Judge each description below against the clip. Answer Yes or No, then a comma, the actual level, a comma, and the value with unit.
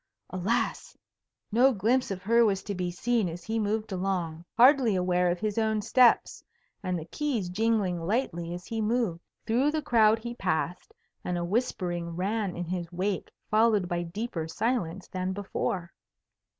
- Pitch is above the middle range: Yes, high, 195 Hz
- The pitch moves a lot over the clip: No, average, 4.4 semitones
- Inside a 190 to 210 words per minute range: No, average, 165 wpm